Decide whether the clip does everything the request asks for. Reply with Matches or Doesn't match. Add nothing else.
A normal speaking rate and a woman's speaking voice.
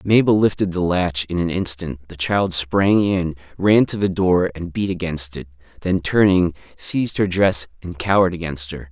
Doesn't match